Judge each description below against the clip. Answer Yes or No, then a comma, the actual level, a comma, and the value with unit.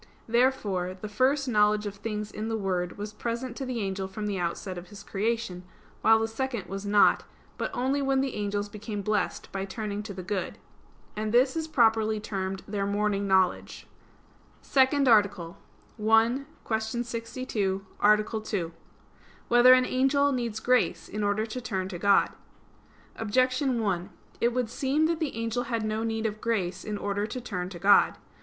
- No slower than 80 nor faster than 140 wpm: No, average, 175 wpm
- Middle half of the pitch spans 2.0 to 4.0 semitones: Yes, average, 3.2 semitones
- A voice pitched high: Yes, high, 215 Hz